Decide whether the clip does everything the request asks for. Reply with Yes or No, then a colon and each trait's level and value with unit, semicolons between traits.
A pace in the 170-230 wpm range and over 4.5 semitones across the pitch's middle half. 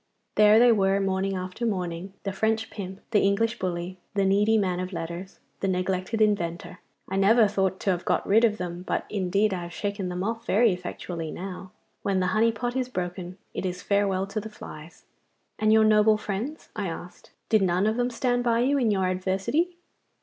No: average, 200 wpm; average, 3.1 semitones